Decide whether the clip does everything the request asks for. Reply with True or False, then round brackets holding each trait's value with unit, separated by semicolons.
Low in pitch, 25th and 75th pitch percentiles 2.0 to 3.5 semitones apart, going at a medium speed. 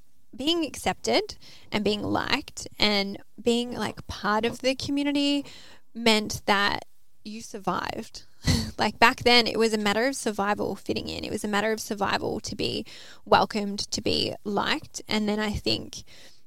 False (225 Hz; 3.2 semitones; 155 wpm)